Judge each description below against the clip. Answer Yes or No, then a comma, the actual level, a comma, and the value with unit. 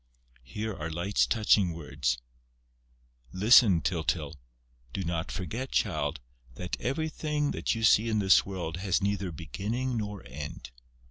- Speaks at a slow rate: Yes, slow, 130 wpm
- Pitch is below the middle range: Yes, very low, 95 Hz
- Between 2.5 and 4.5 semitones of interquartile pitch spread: No, average, 5.3 semitones